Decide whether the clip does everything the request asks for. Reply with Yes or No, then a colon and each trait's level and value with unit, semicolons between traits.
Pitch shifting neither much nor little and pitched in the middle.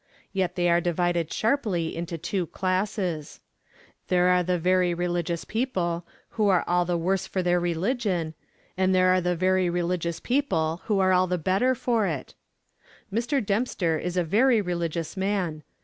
No: narrow, 2.1 semitones; medium, 180 Hz